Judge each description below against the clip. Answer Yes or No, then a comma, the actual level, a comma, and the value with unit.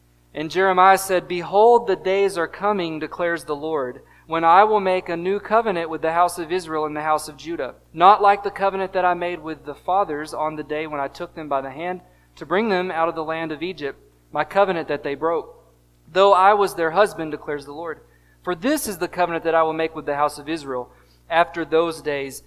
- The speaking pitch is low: No, medium, 165 Hz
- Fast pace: Yes, fast, 230 wpm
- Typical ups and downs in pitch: Yes, average, 3.6 semitones